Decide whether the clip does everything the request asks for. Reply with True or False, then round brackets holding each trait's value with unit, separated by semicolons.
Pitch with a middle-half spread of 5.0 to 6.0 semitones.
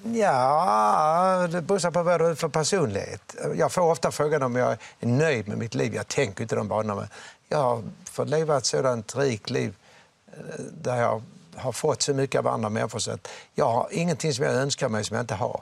True (5.3 semitones)